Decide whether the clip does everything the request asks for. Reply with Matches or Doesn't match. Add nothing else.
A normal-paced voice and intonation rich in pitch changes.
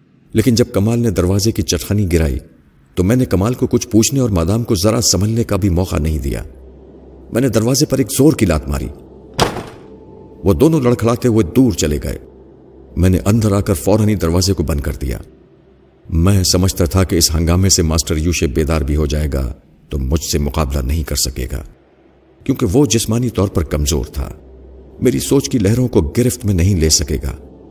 Doesn't match